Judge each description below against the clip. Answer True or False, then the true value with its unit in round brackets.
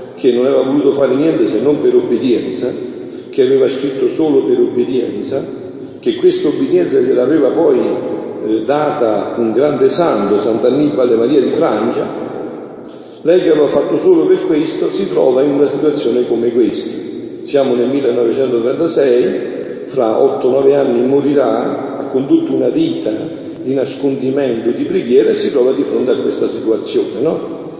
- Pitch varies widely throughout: False (3.3 semitones)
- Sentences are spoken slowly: False (150 wpm)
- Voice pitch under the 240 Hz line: False (365 Hz)